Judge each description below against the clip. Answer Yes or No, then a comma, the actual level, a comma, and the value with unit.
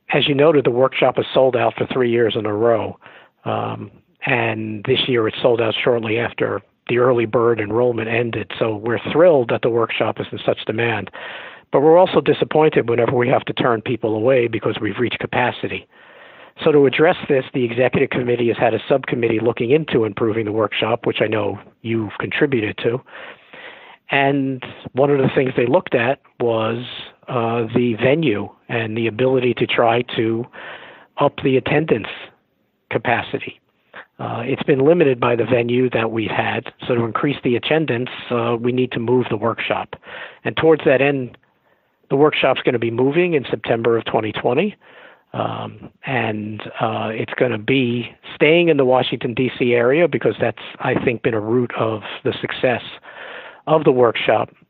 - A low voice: Yes, low, 120 Hz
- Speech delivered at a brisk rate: No, average, 175 wpm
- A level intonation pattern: Yes, narrow, 2.3 semitones